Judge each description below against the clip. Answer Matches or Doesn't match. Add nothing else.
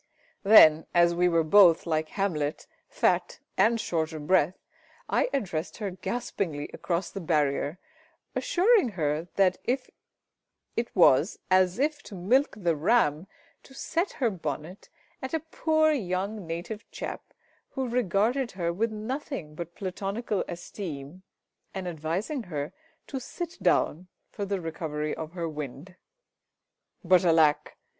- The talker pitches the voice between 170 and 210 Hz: Matches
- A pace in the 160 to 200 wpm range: Doesn't match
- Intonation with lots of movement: Matches